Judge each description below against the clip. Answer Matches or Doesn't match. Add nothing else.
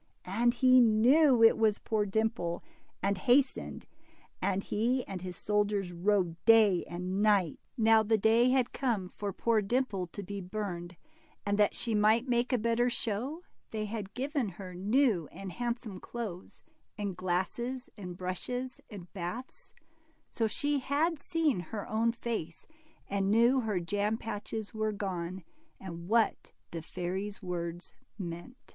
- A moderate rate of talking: Matches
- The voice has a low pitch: Doesn't match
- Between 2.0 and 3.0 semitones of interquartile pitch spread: Doesn't match